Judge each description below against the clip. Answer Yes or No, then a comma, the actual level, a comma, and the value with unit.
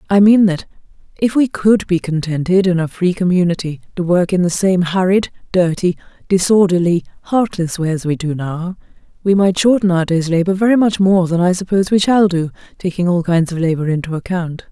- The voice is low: No, medium, 180 Hz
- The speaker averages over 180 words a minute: Yes, average, 195 wpm